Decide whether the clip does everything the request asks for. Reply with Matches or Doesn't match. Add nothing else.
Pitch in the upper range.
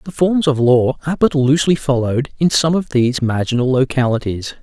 Doesn't match